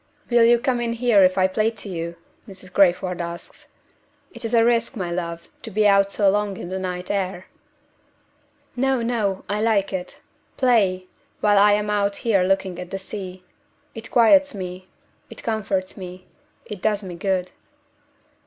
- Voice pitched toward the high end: Yes, high, 200 Hz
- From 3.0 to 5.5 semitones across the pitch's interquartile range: Yes, average, 3.3 semitones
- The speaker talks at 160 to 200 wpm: Yes, average, 170 wpm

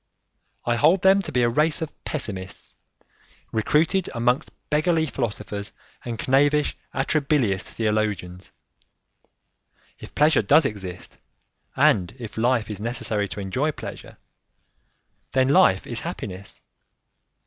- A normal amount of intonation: No, wide, 6.4 semitones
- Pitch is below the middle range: Yes, low, 120 Hz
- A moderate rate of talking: No, slow, 115 wpm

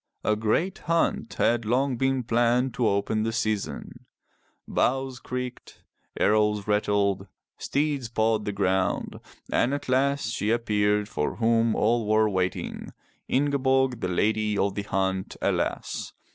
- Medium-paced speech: No, slow, 130 wpm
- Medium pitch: No, low, 110 Hz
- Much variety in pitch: No, average, 3.5 semitones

